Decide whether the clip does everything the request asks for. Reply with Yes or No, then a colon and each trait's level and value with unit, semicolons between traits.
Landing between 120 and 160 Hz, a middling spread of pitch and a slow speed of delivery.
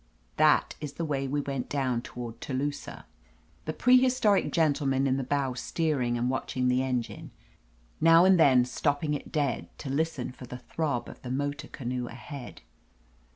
No: low, 135 Hz; average, 3.1 semitones; average, 170 wpm